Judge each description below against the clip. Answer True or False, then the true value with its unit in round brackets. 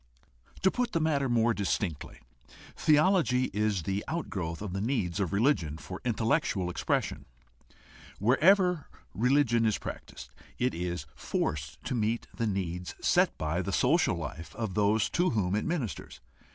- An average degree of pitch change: False (7.1 semitones)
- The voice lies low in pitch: True (110 Hz)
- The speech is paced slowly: False (150 wpm)